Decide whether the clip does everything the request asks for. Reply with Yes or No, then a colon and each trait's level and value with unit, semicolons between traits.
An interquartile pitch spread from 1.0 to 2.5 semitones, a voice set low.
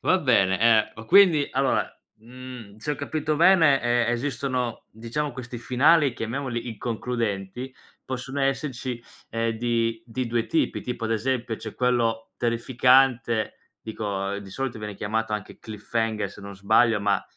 No: average, 2.9 semitones; low, 120 Hz